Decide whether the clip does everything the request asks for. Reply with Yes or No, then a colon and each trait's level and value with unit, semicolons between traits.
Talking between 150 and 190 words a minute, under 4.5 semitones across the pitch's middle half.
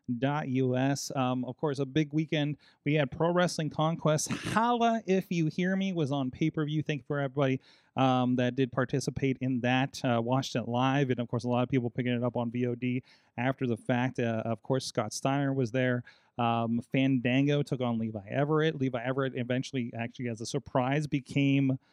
No: average, 200 wpm; average, 2.8 semitones